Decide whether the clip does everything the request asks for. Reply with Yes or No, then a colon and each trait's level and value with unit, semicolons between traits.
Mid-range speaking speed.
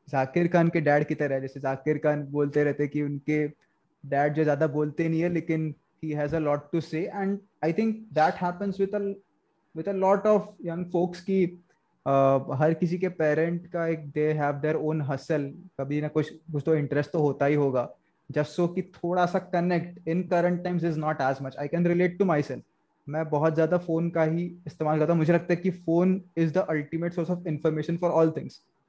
Yes: average, 180 wpm